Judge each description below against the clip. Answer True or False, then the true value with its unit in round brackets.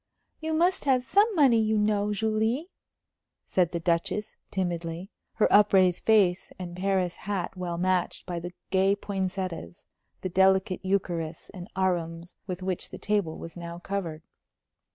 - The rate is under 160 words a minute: True (145 wpm)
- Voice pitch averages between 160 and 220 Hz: True (190 Hz)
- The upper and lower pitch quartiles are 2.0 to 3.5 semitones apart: True (3.0 semitones)